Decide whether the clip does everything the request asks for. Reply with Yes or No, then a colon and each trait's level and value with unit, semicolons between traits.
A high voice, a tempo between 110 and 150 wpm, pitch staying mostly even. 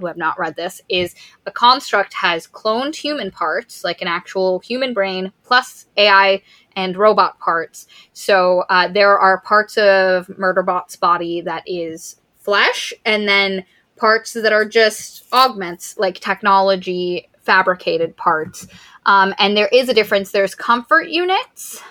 No: high, 195 Hz; average, 145 wpm; average, 3.2 semitones